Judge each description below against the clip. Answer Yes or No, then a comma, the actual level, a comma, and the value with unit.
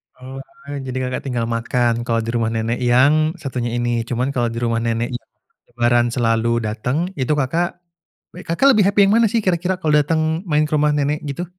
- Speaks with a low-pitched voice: Yes, low, 130 Hz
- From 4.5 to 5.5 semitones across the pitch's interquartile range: Yes, average, 4.9 semitones